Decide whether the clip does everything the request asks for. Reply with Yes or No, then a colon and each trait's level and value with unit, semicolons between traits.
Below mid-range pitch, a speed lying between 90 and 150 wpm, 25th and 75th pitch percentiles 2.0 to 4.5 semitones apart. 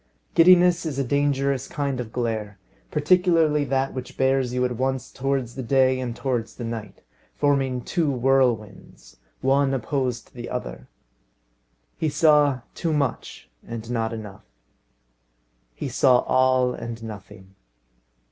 Yes: low, 130 Hz; slow, 135 wpm; average, 2.9 semitones